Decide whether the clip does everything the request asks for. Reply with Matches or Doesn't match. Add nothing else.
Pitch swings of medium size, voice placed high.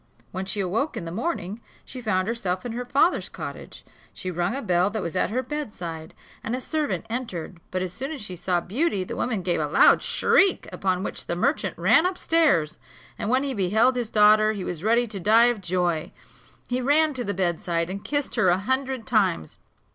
Doesn't match